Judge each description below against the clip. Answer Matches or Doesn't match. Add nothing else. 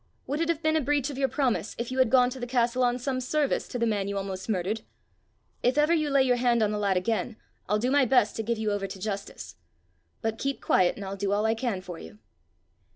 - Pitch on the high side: Matches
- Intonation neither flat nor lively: Matches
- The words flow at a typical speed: Doesn't match